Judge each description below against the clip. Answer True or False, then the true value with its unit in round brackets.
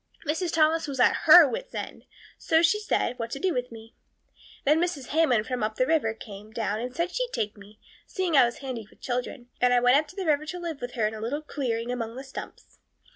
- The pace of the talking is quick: True (235 wpm)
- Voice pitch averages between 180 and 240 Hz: False (255 Hz)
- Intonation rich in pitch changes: True (5.7 semitones)